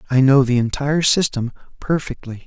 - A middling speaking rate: Yes, average, 145 wpm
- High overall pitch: No, low, 135 Hz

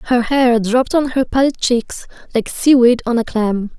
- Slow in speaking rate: No, fast, 205 wpm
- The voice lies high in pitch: Yes, high, 245 Hz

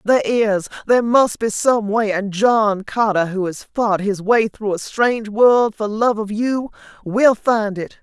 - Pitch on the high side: Yes, high, 215 Hz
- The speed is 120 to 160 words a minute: No, average, 195 wpm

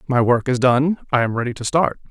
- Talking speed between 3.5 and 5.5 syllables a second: No, 5.7 syllables/s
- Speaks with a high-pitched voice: No, low, 130 Hz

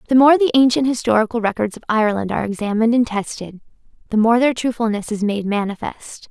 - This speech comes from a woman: Yes, female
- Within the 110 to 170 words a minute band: No, average, 180 wpm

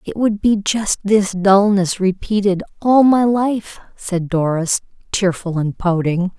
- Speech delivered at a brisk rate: No, average, 140 wpm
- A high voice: Yes, high, 195 Hz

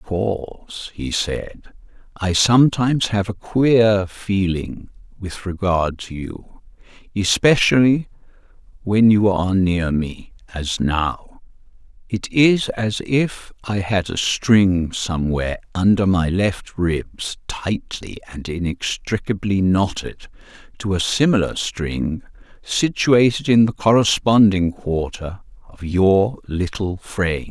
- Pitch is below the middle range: Yes, low, 100 Hz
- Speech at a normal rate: No, slow, 110 wpm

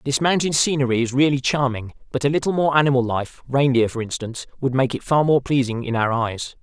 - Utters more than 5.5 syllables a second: Yes, 5.9 syllables/s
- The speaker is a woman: No, male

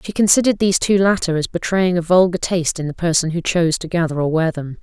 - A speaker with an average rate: No, fast, 250 wpm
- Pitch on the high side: No, medium, 175 Hz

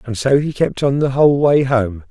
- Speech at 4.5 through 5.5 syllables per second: Yes, 5.1 syllables/s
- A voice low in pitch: Yes, low, 130 Hz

